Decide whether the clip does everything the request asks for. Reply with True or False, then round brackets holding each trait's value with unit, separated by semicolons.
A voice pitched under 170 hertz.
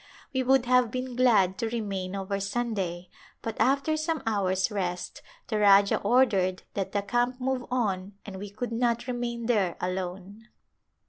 False (215 Hz)